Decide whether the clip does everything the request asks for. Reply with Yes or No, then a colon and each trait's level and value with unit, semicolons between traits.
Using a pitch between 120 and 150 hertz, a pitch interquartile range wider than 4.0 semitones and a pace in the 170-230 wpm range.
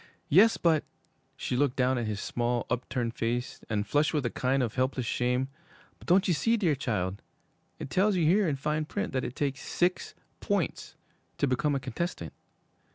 Yes: low, 135 Hz; average, 4.8 semitones; average, 190 wpm